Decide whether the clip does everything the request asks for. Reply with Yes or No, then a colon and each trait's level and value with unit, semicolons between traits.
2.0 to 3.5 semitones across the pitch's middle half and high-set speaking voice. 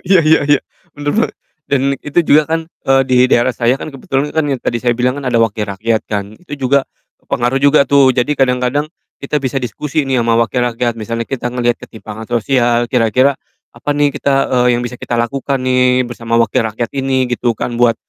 No: average, 2.8 semitones; low, 125 Hz